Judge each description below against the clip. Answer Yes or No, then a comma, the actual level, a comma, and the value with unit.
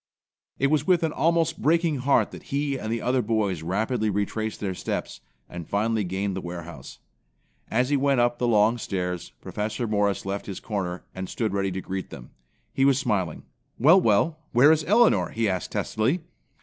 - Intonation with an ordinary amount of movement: No, wide, 6.0 semitones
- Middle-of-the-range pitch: No, low, 110 Hz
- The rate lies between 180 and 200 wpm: Yes, average, 185 wpm